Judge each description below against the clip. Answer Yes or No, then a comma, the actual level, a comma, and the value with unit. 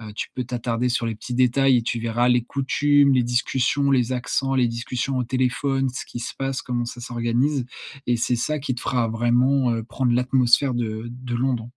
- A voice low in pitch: Yes, low, 125 Hz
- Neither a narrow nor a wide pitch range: No, narrow, 1.9 semitones